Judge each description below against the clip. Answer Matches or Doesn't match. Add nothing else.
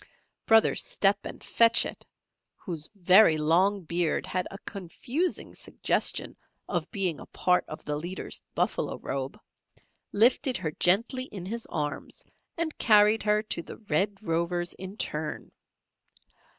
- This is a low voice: Doesn't match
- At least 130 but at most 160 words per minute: Matches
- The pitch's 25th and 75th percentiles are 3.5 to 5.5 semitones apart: Matches